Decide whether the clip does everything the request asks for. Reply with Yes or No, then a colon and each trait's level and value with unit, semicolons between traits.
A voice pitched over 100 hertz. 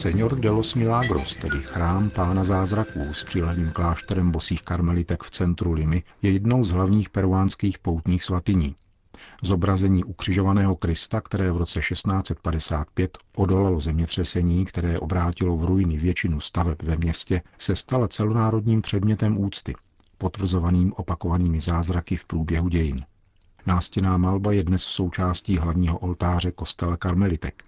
No: very low, 90 Hz